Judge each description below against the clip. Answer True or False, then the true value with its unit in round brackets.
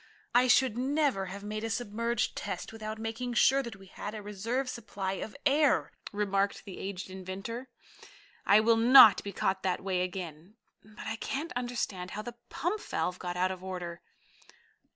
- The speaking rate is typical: True (175 wpm)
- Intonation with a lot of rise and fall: False (4.0 semitones)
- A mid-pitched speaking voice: False (210 Hz)